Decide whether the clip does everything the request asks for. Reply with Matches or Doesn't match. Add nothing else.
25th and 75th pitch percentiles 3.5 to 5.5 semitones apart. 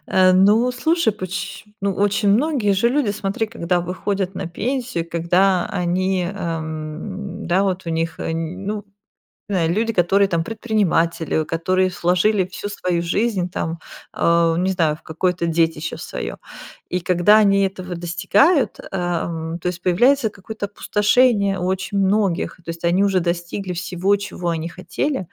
Doesn't match